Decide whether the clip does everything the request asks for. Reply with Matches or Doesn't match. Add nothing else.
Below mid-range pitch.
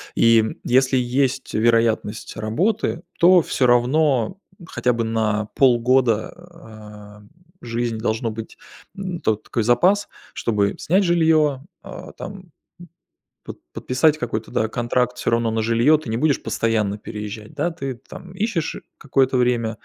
Matches